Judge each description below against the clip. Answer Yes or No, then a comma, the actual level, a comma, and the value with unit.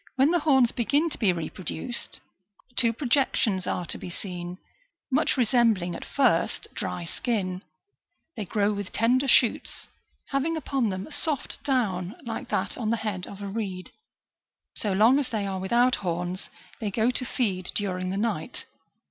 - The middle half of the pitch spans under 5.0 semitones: No, average, 5.3 semitones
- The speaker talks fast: No, average, 165 wpm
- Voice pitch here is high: Yes, high, 215 Hz